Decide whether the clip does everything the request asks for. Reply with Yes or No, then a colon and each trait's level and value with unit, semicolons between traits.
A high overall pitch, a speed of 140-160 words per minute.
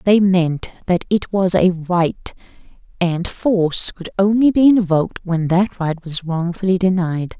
No: medium, 180 Hz; average, 155 wpm